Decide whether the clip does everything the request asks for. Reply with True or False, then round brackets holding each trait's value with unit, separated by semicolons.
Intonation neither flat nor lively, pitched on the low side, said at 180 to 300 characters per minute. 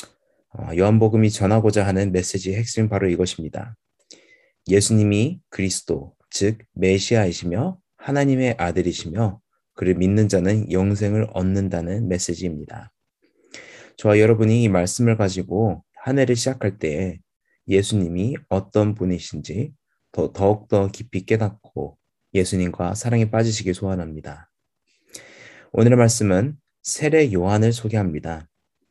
True (3.4 semitones; 100 Hz; 290 characters per minute)